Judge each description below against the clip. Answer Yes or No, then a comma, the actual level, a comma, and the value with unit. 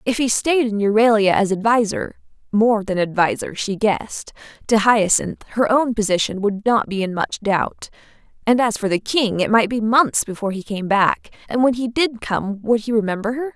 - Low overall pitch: No, high, 220 Hz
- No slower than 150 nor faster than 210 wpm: Yes, average, 190 wpm